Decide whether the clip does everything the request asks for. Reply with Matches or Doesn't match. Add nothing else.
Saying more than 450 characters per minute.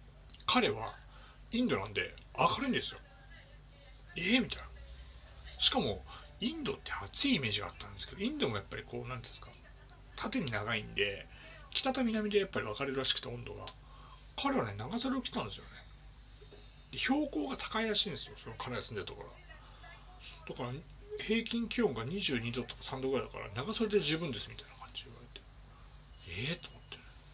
Doesn't match